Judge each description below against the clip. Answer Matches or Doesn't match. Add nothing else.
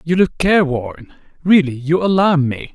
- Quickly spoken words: Doesn't match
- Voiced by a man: Matches